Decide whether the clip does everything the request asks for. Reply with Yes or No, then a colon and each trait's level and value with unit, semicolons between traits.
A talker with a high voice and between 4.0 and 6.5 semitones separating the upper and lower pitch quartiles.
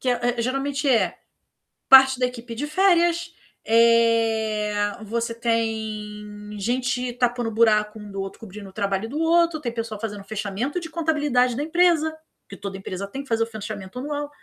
Yes: high, 230 Hz; average, 4.4 semitones